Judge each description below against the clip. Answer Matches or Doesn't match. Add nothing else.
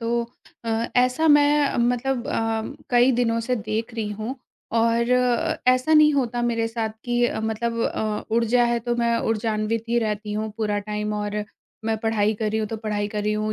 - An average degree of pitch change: Doesn't match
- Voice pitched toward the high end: Matches